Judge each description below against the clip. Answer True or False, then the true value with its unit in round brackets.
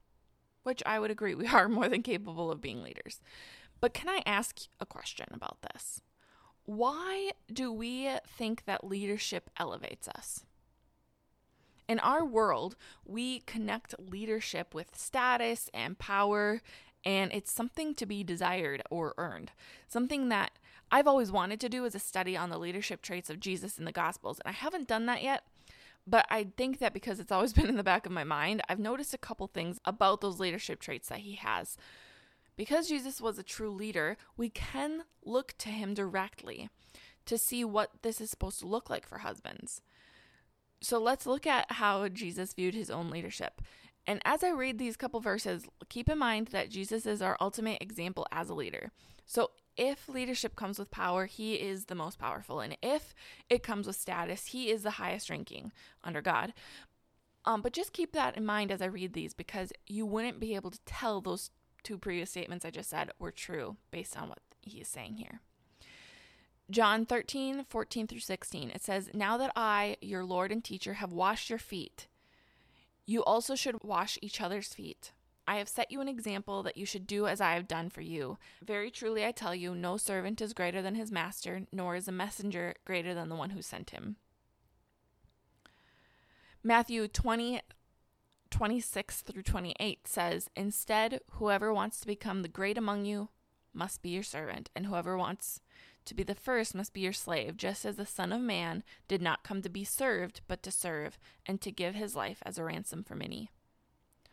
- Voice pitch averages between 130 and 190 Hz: False (205 Hz)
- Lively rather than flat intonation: False (3.6 semitones)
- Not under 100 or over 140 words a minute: False (185 wpm)